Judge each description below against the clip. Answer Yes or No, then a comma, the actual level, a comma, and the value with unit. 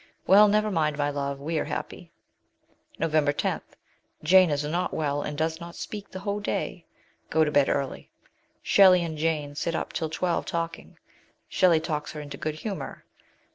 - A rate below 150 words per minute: No, average, 175 wpm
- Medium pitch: Yes, medium, 160 Hz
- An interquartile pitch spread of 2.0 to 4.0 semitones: Yes, average, 3.5 semitones